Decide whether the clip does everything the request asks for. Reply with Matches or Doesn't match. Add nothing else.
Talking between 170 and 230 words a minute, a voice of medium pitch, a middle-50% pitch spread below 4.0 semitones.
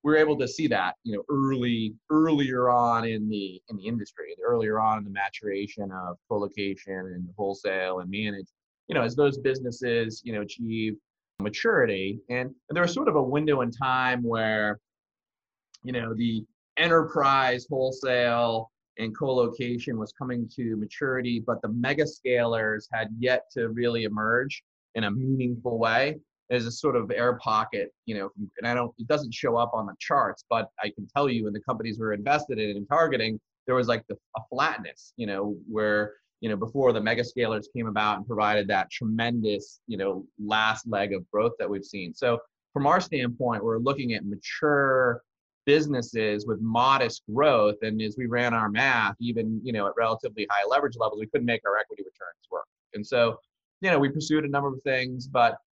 Doesn't match